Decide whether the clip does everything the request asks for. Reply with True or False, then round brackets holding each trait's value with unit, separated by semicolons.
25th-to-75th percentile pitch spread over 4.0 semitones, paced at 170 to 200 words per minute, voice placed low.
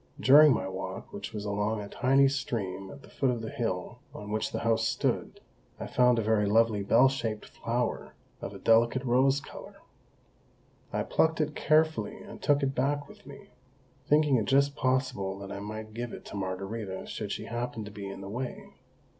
True (4.8 semitones; 195 wpm; 115 Hz)